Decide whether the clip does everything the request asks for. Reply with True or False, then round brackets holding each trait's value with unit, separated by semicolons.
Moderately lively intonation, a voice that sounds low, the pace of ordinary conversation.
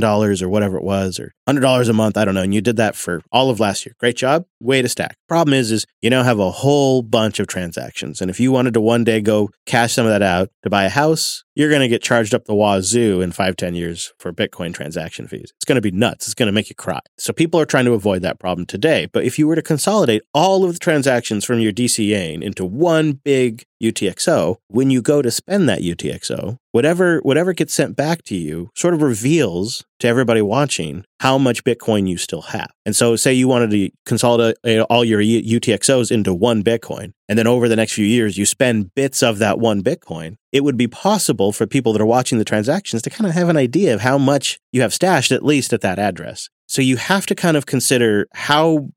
False (4.8 semitones; 120 Hz; 245 wpm)